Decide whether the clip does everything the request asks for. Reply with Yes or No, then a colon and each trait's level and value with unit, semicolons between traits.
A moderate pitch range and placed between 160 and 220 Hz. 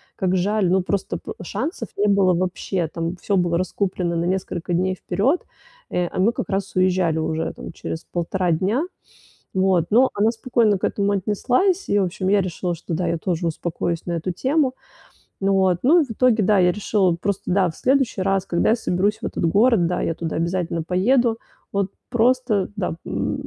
Yes: average, 3.2 semitones; high, 190 Hz